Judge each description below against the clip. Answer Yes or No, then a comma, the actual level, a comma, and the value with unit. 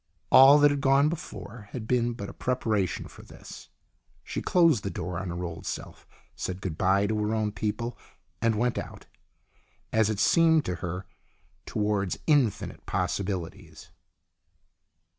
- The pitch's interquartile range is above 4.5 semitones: Yes, average, 4.9 semitones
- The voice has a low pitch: Yes, low, 105 Hz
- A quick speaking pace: No, average, 150 wpm